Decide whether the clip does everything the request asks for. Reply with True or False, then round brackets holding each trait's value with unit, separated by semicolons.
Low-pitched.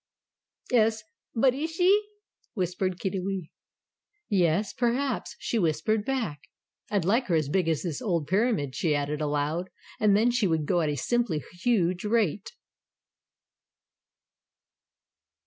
False (190 Hz)